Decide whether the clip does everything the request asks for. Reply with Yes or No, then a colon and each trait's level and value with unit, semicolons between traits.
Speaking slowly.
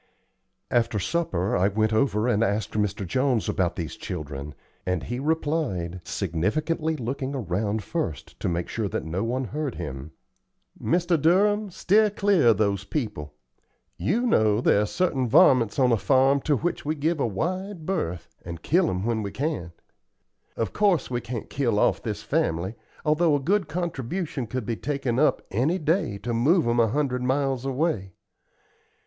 No: average, 165 wpm